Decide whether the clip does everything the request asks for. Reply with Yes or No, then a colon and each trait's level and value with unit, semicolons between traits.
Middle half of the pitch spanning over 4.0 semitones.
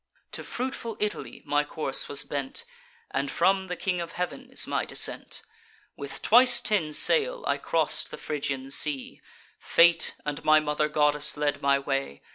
Yes: average, 5.0 semitones